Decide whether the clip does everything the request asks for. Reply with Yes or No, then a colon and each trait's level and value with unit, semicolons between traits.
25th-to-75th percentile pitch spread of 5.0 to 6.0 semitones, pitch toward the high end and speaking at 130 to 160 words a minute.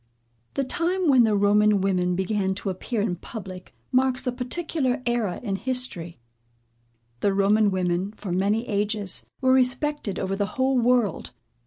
No: average, 4.6 semitones; high, 210 Hz; average, 150 wpm